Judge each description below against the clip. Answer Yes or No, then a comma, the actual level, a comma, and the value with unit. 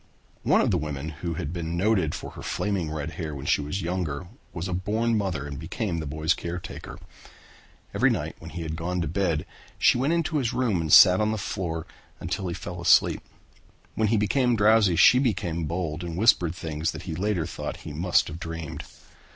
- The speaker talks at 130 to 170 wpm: No, fast, 205 wpm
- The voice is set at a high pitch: No, very low, 85 Hz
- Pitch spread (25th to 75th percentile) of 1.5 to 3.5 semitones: No, average, 4.2 semitones